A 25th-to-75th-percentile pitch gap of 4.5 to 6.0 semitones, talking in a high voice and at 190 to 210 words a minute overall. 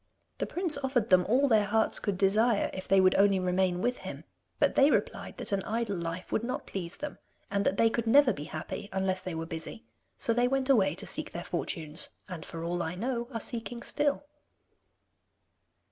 Yes: average, 4.8 semitones; high, 205 Hz; fast, 205 wpm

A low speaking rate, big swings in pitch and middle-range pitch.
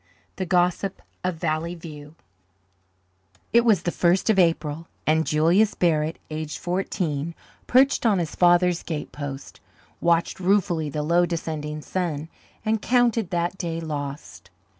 No: slow, 130 wpm; average, 3.1 semitones; medium, 170 Hz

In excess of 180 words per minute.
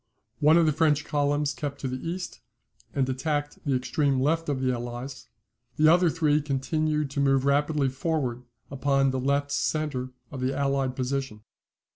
No: average, 165 wpm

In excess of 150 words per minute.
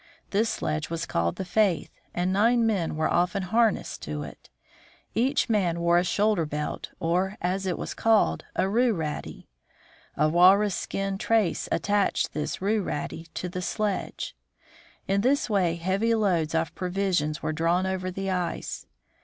Yes: average, 165 wpm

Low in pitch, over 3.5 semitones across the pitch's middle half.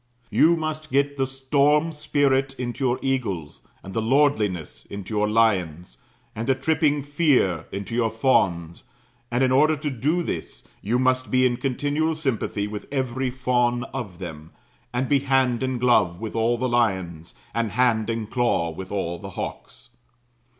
Yes: low, 125 Hz; average, 4.6 semitones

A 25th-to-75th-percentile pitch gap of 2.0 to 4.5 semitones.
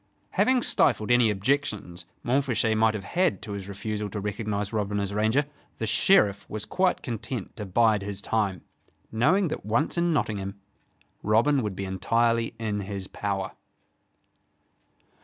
Yes: average, 2.9 semitones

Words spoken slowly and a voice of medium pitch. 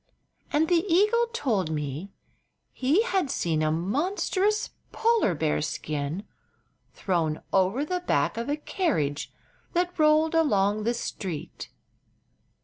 No: slow, 120 wpm; very high, 250 Hz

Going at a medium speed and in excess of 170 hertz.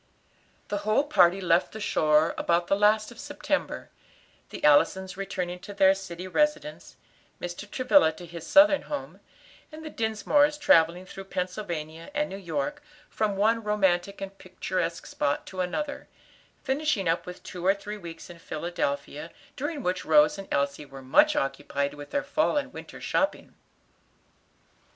Yes: average, 155 wpm; high, 190 Hz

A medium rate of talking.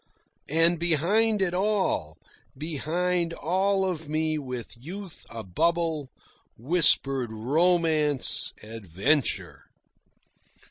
No: slow, 80 wpm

